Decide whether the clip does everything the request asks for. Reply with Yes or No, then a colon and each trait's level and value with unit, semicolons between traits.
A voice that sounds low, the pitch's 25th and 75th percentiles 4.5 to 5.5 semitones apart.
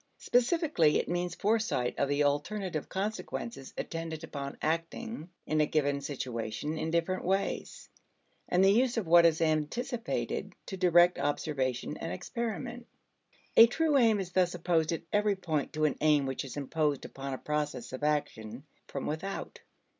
No: medium, 165 Hz; average, 5.1 semitones